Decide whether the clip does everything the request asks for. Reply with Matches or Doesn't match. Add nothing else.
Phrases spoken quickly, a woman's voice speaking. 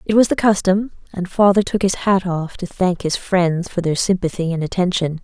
Matches